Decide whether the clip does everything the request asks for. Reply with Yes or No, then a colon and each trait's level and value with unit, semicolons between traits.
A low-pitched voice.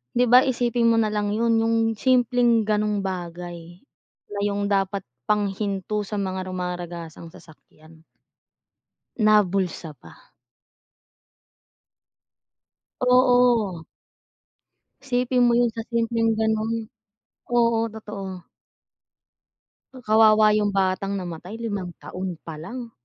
No: high, 210 Hz